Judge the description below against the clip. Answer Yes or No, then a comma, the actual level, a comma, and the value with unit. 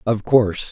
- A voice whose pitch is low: Yes, low, 110 Hz